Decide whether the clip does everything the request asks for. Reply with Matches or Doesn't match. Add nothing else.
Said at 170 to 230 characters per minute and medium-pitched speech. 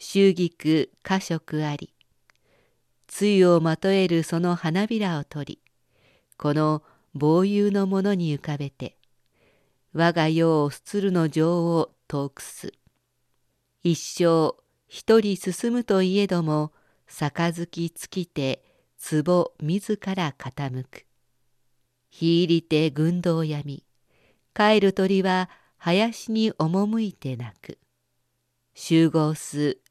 Matches